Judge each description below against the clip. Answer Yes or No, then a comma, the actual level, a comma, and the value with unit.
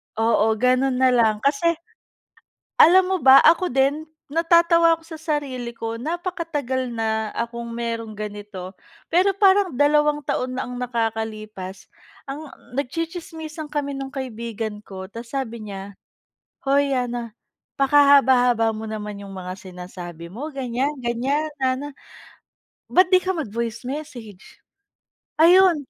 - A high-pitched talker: Yes, very high, 255 Hz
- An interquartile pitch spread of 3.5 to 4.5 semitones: No, average, 5.2 semitones